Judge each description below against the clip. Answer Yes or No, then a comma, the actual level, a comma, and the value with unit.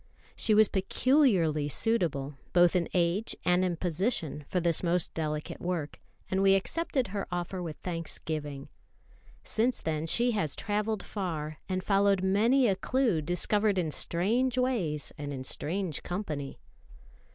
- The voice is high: No, medium, 180 Hz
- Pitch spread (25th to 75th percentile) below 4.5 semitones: No, average, 4.9 semitones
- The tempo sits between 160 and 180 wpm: No, average, 140 wpm